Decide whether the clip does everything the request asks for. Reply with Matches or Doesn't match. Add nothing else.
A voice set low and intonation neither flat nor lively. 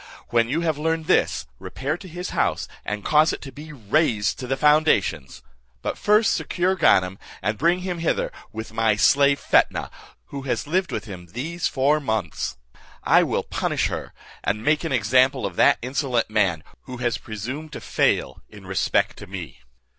Doesn't match